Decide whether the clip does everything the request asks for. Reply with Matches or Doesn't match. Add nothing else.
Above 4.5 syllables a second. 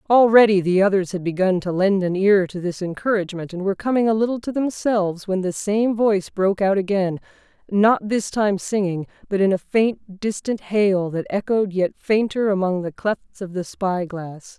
Matches